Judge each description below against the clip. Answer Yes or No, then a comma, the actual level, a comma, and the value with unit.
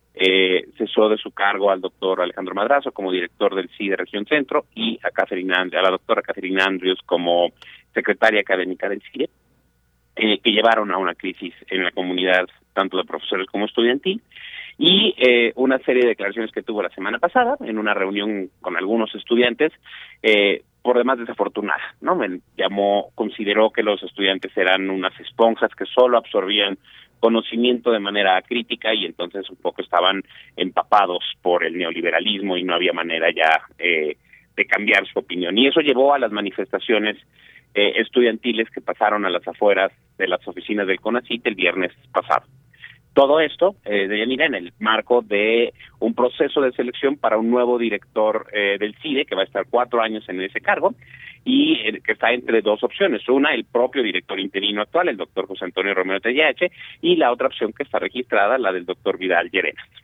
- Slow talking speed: No, average, 180 wpm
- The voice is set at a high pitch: No, low, 105 Hz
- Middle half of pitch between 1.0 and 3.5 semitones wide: No, average, 4.3 semitones